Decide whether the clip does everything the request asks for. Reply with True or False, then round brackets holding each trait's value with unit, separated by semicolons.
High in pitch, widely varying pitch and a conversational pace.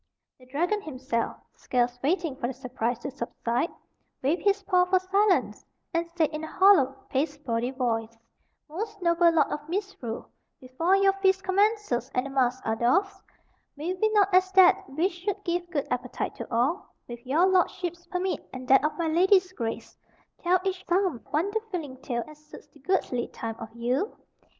True (320 Hz; 6.6 semitones; 175 wpm)